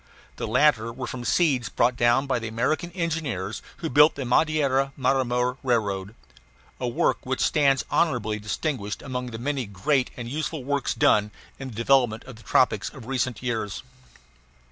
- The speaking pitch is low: Yes, low, 125 Hz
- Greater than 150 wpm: Yes, average, 165 wpm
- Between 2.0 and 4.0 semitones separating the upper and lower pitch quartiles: Yes, average, 3.4 semitones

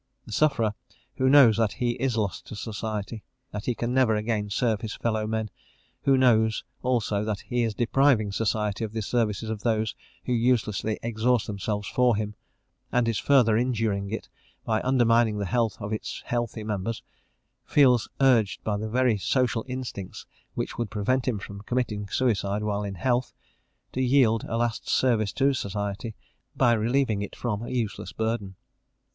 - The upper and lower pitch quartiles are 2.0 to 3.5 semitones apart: Yes, average, 2.7 semitones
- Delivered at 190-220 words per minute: No, average, 170 wpm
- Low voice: Yes, low, 110 Hz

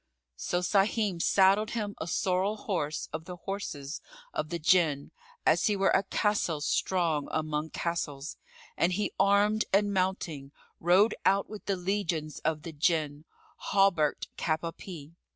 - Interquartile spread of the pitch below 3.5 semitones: No, average, 4.1 semitones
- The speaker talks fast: No, average, 150 wpm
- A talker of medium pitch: Yes, medium, 175 Hz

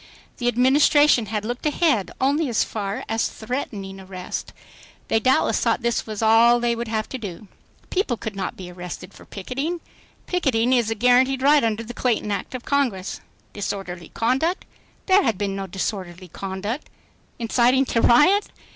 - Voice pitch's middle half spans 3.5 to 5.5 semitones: Yes, average, 4.6 semitones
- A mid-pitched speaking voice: No, high, 230 Hz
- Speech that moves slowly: No, average, 165 wpm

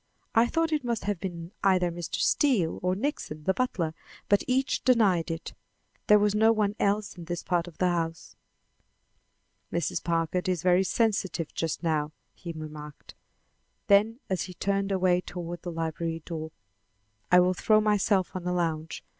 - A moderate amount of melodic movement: Yes, average, 3.6 semitones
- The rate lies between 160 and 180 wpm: Yes, average, 165 wpm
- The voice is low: No, medium, 180 Hz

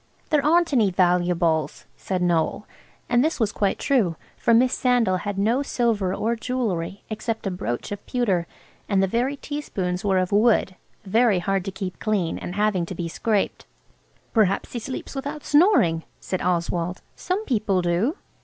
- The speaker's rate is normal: Yes, average, 165 wpm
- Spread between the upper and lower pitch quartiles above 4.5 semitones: Yes, average, 5.2 semitones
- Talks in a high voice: Yes, high, 200 Hz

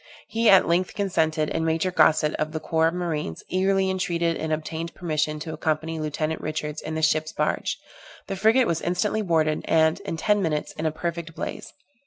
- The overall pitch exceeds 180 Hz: No, medium, 160 Hz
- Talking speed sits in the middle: Yes, average, 190 wpm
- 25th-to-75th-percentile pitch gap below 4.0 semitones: Yes, average, 2.7 semitones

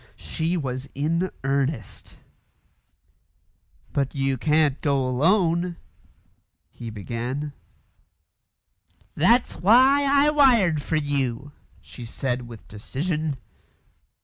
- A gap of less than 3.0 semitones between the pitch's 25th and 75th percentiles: No, average, 5.1 semitones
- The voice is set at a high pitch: No, medium, 145 Hz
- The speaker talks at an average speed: No, slow, 95 wpm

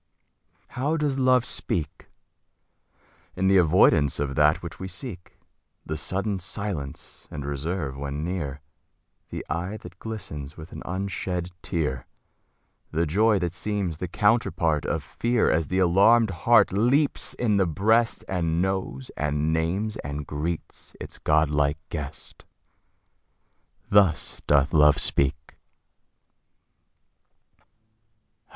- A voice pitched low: Yes, very low, 85 Hz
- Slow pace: Yes, slow, 120 wpm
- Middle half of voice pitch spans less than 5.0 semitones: No, average, 5.3 semitones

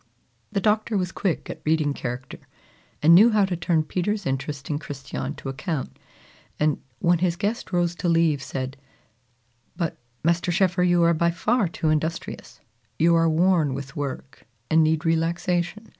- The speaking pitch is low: No, medium, 165 Hz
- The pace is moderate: Yes, average, 160 wpm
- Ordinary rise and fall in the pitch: Yes, average, 3.1 semitones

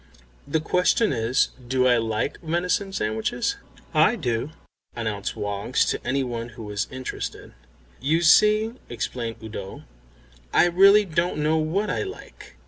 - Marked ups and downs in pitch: Yes, wide, 7.5 semitones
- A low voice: Yes, low, 130 Hz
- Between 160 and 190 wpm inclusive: No, slow, 135 wpm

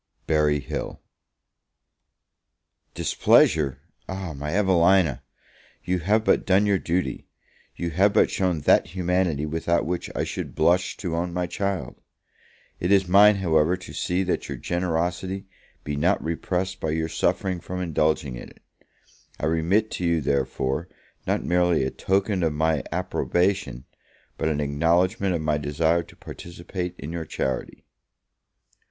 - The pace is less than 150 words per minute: Yes, average, 140 wpm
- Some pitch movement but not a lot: Yes, average, 3.1 semitones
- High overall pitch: No, very low, 85 Hz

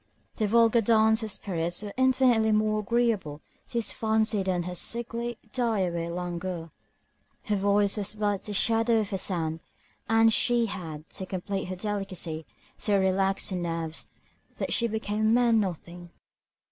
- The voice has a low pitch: No, high, 205 Hz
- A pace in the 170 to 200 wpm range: No, average, 160 wpm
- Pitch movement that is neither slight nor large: Yes, average, 3.8 semitones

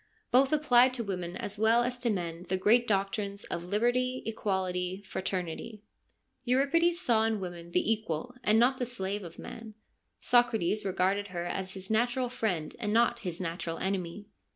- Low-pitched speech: No, high, 210 Hz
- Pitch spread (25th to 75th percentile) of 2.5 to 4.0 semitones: No, average, 4.6 semitones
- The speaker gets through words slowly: No, average, 165 wpm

